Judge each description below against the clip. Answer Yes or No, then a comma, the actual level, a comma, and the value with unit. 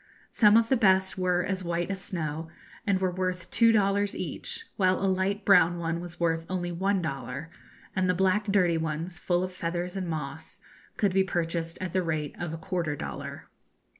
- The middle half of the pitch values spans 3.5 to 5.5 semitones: No, narrow, 2.4 semitones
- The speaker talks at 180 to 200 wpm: Yes, average, 195 wpm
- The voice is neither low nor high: Yes, medium, 180 Hz